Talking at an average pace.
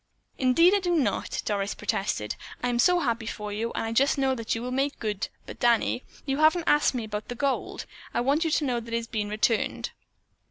No: fast, 225 wpm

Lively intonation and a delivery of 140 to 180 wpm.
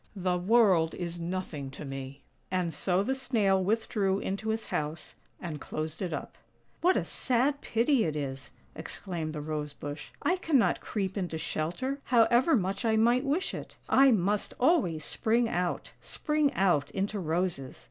Yes: wide, 6.6 semitones; average, 160 wpm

